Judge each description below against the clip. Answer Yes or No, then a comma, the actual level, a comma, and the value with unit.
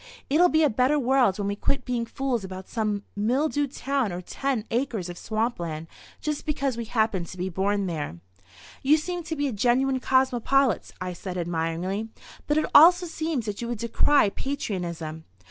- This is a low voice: No, high, 235 Hz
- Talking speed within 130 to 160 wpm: No, average, 180 wpm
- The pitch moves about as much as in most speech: No, wide, 6.5 semitones